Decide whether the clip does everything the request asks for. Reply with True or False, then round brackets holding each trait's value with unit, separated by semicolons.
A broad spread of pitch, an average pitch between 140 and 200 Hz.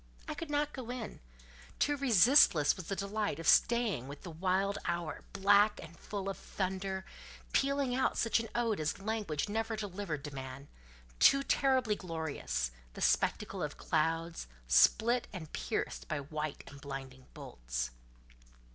True (6.9 semitones; 190 Hz)